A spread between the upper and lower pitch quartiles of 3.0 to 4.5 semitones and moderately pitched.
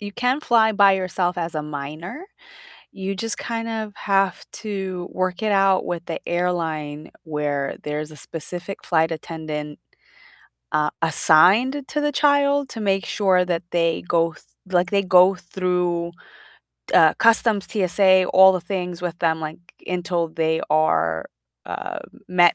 Yes: average, 3.5 semitones; medium, 180 Hz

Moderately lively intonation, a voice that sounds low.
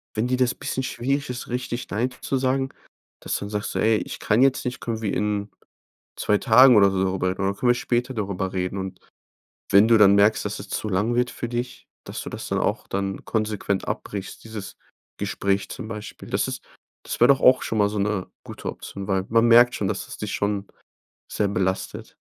Yes: average, 3.6 semitones; low, 105 Hz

